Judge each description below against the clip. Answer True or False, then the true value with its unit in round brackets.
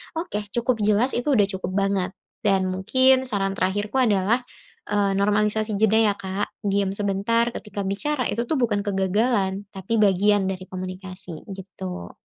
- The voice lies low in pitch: False (205 Hz)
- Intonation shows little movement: True (2.3 semitones)